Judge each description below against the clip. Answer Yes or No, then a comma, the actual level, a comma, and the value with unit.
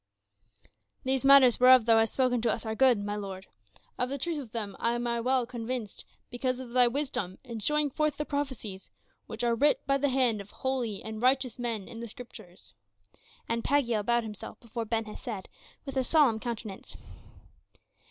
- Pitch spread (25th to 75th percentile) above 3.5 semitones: No, average, 3.0 semitones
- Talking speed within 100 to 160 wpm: No, average, 180 wpm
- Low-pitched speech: No, high, 240 Hz